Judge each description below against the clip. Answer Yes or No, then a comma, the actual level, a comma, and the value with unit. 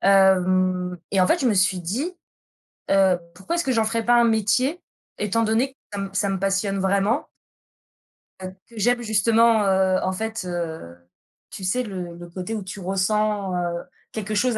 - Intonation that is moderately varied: Yes, average, 3.2 semitones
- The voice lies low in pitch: No, high, 195 Hz